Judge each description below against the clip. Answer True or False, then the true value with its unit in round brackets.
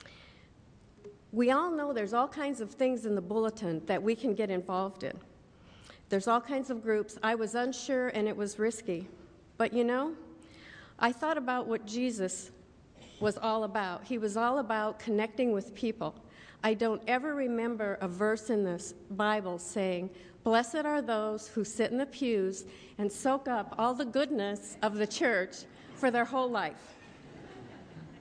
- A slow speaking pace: False (165 wpm)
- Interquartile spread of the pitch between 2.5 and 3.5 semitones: True (3.1 semitones)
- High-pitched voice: True (220 Hz)